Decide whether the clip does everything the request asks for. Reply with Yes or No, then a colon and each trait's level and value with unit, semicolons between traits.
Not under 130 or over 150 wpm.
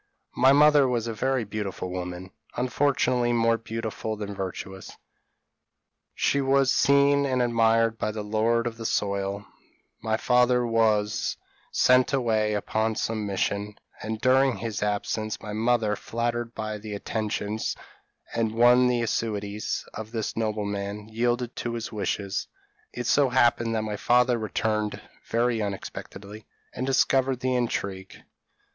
Yes: average, 140 wpm